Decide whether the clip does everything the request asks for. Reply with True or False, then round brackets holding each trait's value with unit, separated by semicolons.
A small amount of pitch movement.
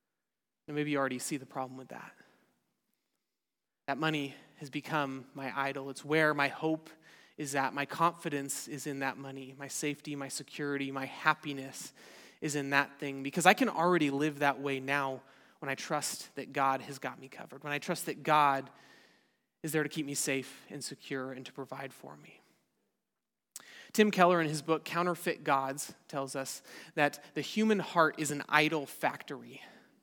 True (2.3 semitones)